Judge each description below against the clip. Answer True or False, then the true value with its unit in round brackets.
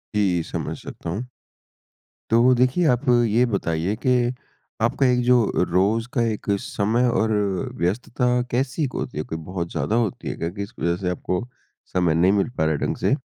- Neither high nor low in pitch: False (105 Hz)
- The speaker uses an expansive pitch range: True (5.8 semitones)